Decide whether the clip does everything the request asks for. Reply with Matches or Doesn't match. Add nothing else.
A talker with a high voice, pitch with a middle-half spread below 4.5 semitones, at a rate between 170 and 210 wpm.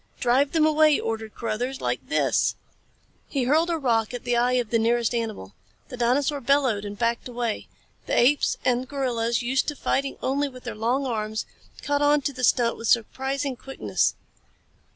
Matches